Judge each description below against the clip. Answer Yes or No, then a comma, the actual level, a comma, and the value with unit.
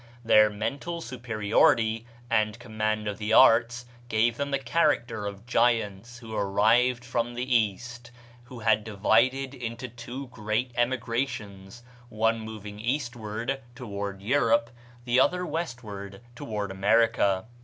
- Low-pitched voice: Yes, low, 115 Hz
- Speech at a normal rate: No, slow, 125 wpm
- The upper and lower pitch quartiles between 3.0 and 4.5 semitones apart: No, narrow, 2.4 semitones